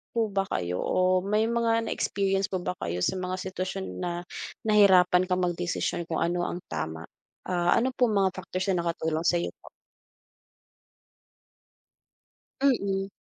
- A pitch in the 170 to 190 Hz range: Yes, medium, 185 Hz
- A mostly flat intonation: Yes, narrow, 2.1 semitones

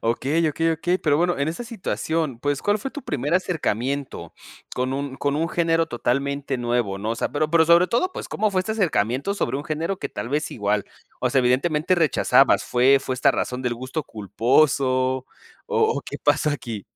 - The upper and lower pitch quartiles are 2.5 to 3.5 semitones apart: No, average, 4.8 semitones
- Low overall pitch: No, medium, 145 Hz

